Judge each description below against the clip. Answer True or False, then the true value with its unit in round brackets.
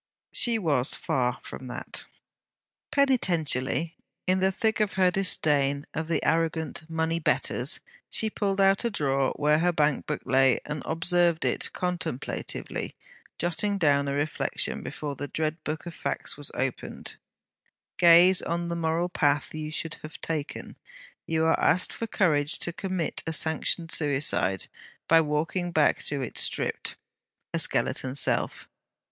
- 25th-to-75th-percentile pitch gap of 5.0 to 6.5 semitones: False (3.3 semitones)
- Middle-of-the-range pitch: True (160 Hz)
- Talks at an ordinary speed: True (145 wpm)